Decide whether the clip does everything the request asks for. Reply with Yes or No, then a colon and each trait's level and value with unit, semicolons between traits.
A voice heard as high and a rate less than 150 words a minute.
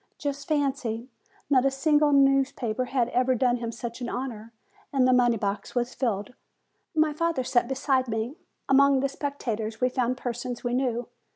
No: very high, 255 Hz; average, 175 wpm